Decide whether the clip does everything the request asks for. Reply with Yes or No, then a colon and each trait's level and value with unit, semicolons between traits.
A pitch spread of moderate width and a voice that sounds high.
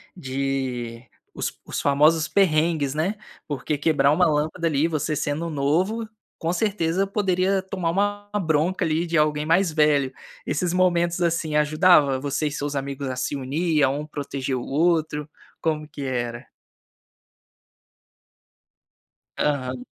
No: average, 3.5 semitones; medium, 155 Hz